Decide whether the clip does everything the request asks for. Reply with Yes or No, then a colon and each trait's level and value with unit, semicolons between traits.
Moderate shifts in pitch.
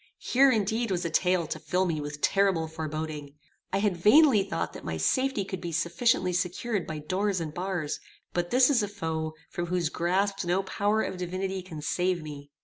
Yes: average, 3.8 semitones